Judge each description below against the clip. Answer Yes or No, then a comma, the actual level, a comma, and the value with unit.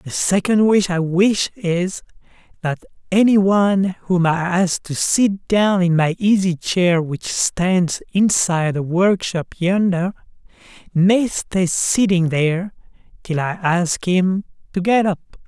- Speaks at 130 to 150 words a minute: Yes, average, 140 wpm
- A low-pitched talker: No, medium, 185 Hz